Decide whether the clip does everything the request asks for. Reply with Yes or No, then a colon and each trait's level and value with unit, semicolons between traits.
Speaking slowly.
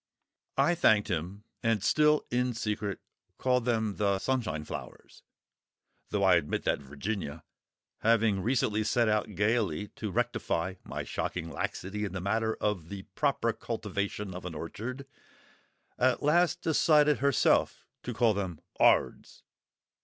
Yes: slow, 130 wpm